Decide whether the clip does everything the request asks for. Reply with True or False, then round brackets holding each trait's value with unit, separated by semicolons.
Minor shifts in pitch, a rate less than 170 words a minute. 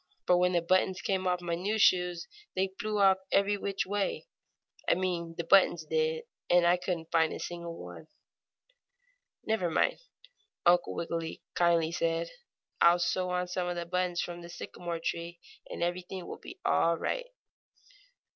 True (1.5 semitones; 160 wpm)